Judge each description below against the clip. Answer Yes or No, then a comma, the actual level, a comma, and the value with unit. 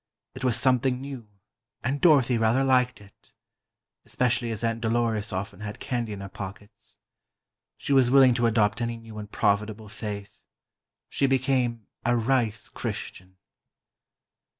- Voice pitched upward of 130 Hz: No, low, 115 Hz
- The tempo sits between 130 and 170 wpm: Yes, average, 140 wpm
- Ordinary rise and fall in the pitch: Yes, average, 3.2 semitones